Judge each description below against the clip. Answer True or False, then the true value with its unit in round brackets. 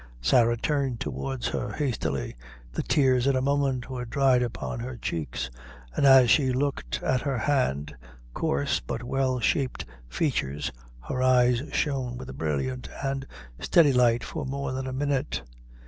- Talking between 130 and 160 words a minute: True (155 wpm)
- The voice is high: False (125 Hz)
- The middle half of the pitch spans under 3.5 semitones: True (3.0 semitones)